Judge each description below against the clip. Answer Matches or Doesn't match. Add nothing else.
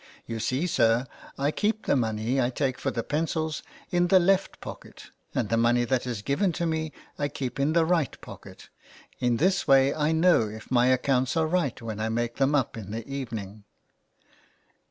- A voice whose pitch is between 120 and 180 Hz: Matches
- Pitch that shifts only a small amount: Doesn't match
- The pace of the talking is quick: Doesn't match